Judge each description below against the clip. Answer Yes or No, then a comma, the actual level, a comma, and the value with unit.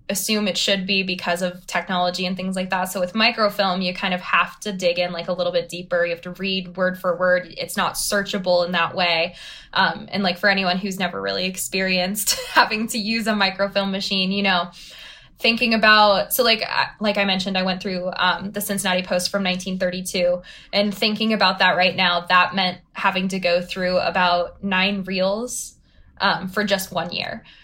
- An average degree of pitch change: No, narrow, 1.7 semitones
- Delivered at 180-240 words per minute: Yes, average, 200 wpm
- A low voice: No, medium, 185 Hz